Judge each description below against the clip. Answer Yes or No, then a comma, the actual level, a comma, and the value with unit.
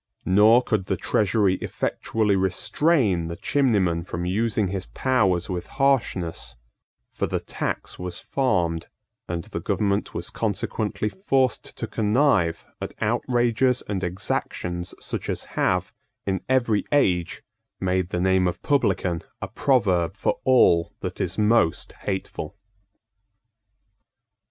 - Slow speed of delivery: Yes, slow, 120 wpm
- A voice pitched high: No, very low, 95 Hz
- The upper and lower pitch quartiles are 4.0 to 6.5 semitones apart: Yes, average, 4.9 semitones